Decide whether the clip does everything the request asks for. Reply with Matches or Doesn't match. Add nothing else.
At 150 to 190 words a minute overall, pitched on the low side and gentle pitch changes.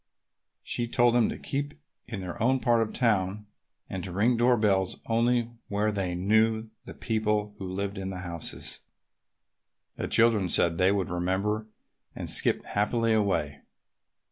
Doesn't match